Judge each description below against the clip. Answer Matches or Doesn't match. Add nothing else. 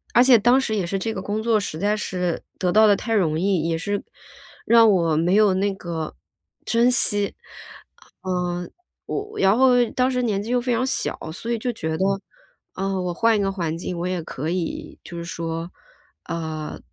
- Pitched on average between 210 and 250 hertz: Doesn't match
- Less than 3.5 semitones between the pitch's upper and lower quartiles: Doesn't match